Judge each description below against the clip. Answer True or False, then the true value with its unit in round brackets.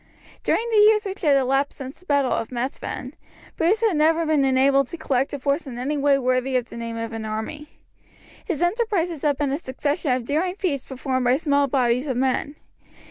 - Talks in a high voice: True (280 Hz)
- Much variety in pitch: False (3.8 semitones)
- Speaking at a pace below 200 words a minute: False (205 wpm)